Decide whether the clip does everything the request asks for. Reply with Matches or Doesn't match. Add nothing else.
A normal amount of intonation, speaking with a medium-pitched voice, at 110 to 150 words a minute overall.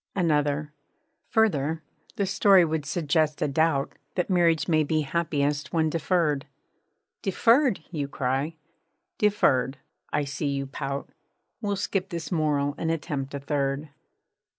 Matches